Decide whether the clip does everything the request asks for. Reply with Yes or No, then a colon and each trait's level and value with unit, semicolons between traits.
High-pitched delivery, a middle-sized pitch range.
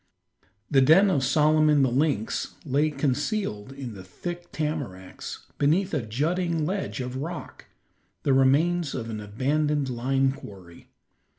No: medium, 140 Hz; average, 3.8 semitones